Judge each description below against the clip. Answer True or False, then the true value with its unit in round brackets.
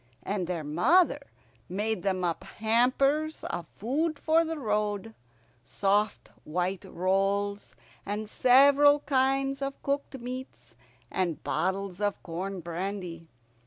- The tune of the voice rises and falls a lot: True (6.5 semitones)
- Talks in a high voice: True (210 Hz)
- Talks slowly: True (115 wpm)